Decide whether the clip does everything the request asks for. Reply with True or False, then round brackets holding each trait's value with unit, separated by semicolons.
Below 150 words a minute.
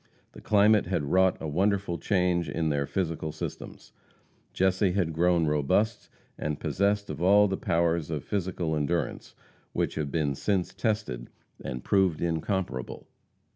True (135 wpm)